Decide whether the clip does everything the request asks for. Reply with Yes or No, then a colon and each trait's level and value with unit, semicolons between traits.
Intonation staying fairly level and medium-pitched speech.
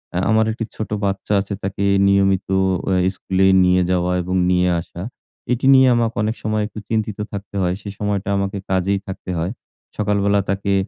No: narrow, 2.2 semitones; low, 100 Hz